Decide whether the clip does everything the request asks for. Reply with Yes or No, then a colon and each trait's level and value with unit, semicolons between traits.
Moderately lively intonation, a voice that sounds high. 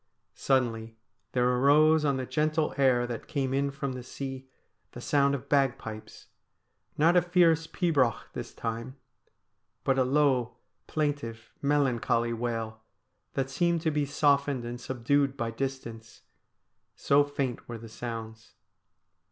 No: average, 3.3 semitones; low, 135 Hz